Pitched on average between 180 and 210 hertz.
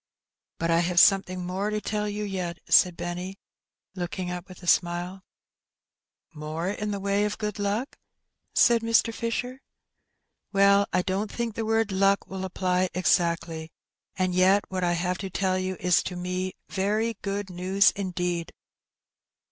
Yes: high, 190 Hz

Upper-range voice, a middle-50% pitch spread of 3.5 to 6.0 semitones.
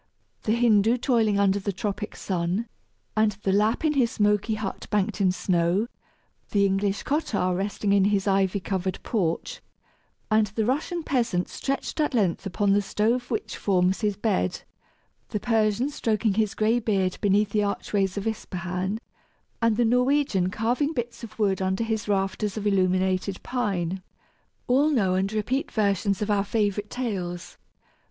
No: high, 205 Hz; average, 2.9 semitones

